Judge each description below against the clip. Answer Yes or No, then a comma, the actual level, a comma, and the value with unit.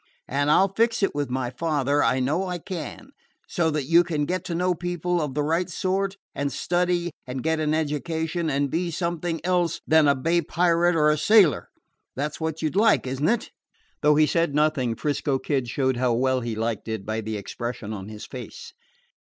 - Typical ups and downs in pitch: Yes, average, 4.7 semitones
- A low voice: No, medium, 155 Hz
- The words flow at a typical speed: No, fast, 210 wpm